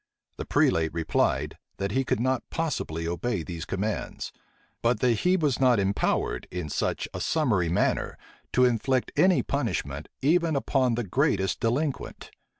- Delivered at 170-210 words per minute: No, average, 150 wpm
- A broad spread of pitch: Yes, wide, 6.8 semitones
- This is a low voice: Yes, low, 120 Hz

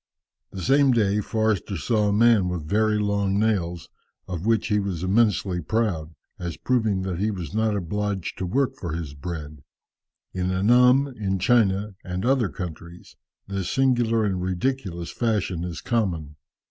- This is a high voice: No, low, 100 Hz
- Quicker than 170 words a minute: No, average, 155 wpm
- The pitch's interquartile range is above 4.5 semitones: No, average, 3.9 semitones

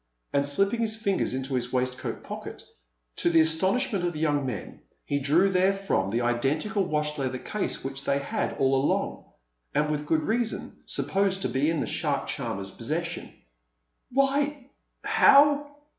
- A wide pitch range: Yes, wide, 6.8 semitones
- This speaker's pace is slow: No, average, 160 wpm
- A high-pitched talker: No, medium, 160 Hz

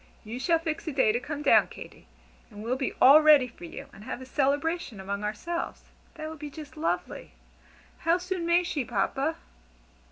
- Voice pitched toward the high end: Yes, very high, 285 Hz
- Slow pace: No, average, 190 wpm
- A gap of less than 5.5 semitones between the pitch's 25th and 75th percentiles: Yes, average, 5.1 semitones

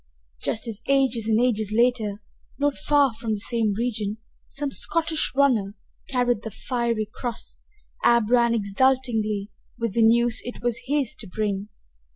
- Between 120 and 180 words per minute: Yes, average, 150 wpm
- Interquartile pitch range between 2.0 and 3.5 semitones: Yes, average, 2.7 semitones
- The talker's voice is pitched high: Yes, high, 235 Hz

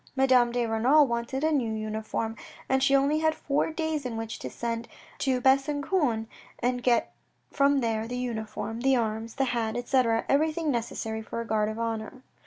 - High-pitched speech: Yes, high, 245 Hz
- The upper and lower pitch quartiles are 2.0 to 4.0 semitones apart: Yes, average, 3.5 semitones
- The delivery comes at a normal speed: Yes, average, 180 wpm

